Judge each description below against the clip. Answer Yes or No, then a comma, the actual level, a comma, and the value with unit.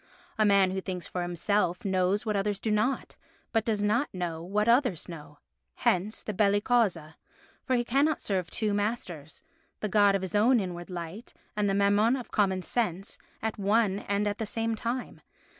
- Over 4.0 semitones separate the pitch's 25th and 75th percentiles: No, average, 3.1 semitones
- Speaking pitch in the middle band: No, high, 205 Hz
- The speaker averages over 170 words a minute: Yes, average, 180 wpm